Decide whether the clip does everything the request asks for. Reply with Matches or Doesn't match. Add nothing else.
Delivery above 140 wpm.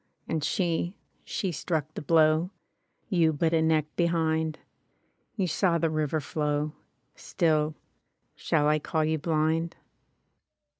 Doesn't match